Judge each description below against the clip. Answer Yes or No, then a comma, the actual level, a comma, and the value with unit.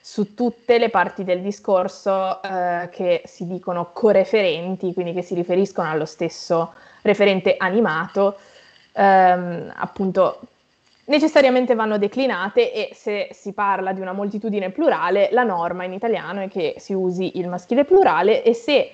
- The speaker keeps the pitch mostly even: No, average, 4.4 semitones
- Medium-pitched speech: No, high, 195 Hz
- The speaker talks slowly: No, average, 145 wpm